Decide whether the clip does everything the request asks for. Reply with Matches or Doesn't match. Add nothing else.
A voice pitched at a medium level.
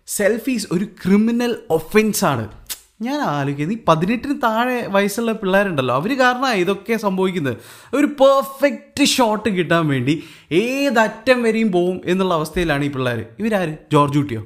Doesn't match